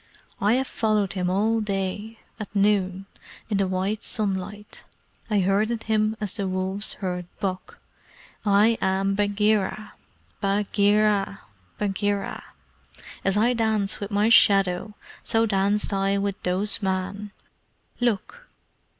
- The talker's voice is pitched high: Yes, high, 205 Hz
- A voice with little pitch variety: Yes, narrow, 1.7 semitones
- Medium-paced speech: No, slow, 120 wpm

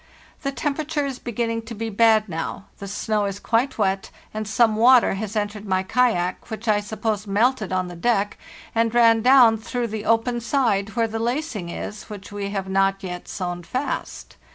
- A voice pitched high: Yes, high, 220 Hz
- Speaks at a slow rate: No, average, 185 wpm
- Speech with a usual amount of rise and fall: Yes, average, 3.0 semitones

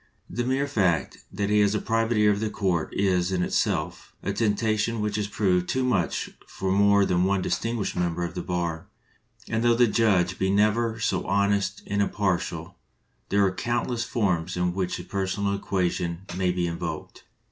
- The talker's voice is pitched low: Yes, low, 100 Hz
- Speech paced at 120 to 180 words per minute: No, average, 190 wpm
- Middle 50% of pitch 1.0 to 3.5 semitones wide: Yes, average, 3.1 semitones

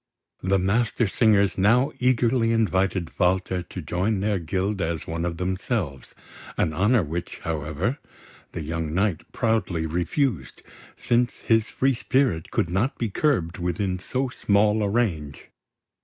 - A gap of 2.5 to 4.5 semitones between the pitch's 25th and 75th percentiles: No, average, 5.0 semitones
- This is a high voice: No, very low, 95 Hz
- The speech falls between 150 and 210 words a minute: No, slow, 135 wpm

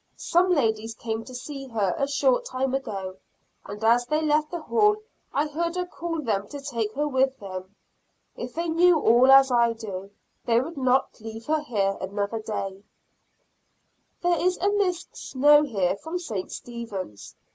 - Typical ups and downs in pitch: No, wide, 6.0 semitones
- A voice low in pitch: No, very high, 260 Hz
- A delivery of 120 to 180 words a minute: Yes, average, 170 wpm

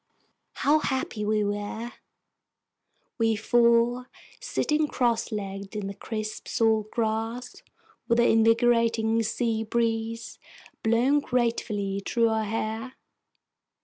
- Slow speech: Yes, slow, 100 wpm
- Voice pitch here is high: Yes, high, 225 Hz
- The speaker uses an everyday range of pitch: No, narrow, 1.6 semitones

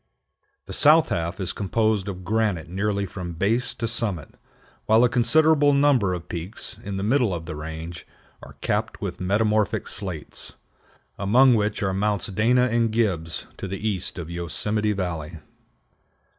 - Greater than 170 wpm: No, average, 155 wpm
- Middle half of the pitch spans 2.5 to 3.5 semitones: No, average, 4.2 semitones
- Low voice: Yes, low, 100 Hz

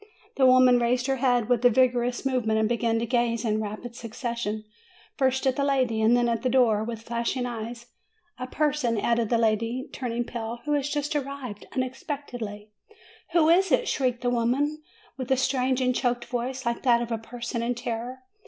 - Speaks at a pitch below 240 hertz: No, high, 245 Hz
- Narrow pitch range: Yes, narrow, 2.0 semitones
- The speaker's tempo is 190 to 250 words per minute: Yes, average, 195 wpm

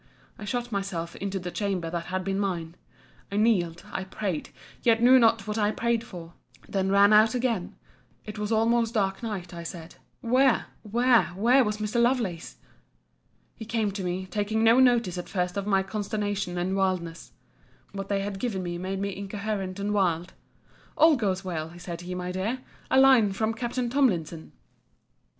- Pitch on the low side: No, high, 200 Hz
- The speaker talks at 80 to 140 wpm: No, average, 170 wpm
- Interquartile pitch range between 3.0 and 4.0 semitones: Yes, average, 3.7 semitones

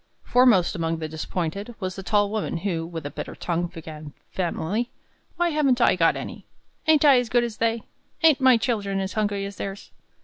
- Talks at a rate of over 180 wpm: Yes, average, 195 wpm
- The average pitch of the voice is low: No, high, 200 Hz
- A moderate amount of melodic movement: No, wide, 6.0 semitones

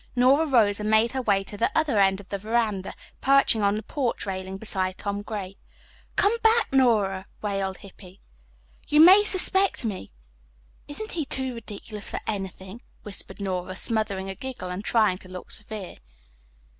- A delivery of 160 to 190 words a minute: Yes, average, 165 wpm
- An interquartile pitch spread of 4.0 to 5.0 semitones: Yes, average, 4.7 semitones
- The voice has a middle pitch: No, high, 210 Hz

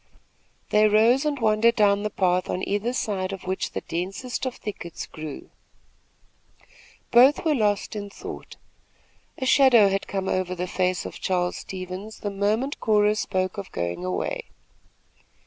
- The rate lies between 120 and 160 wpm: Yes, average, 150 wpm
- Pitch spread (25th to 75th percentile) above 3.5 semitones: No, average, 3.0 semitones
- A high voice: Yes, high, 200 Hz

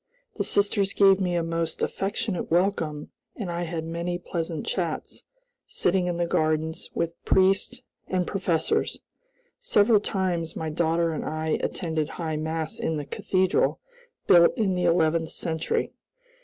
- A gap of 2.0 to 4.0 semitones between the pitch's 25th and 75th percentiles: Yes, average, 2.7 semitones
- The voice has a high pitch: No, medium, 170 Hz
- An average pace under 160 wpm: Yes, average, 145 wpm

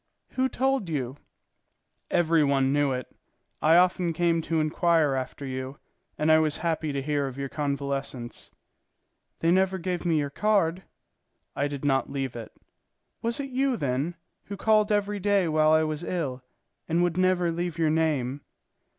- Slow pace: No, average, 165 wpm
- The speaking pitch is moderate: Yes, medium, 160 Hz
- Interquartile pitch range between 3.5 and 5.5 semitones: Yes, average, 4.2 semitones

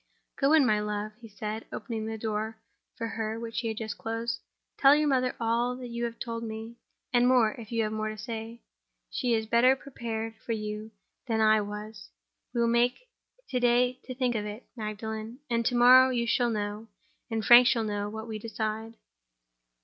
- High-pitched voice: Yes, high, 225 Hz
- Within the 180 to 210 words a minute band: Yes, average, 190 wpm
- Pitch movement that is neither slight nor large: No, narrow, 1.9 semitones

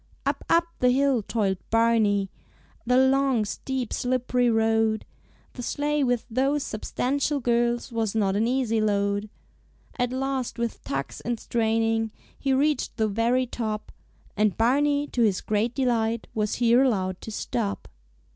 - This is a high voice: Yes, high, 235 Hz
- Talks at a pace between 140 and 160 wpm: Yes, average, 145 wpm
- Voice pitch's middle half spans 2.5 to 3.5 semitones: Yes, average, 2.9 semitones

